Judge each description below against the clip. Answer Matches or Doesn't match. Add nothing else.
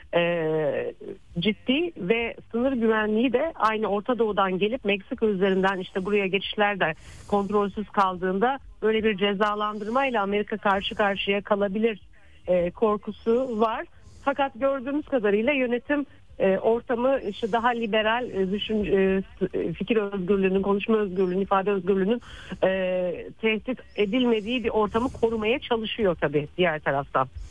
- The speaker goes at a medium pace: Matches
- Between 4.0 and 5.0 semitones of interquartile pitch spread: Doesn't match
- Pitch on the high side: Matches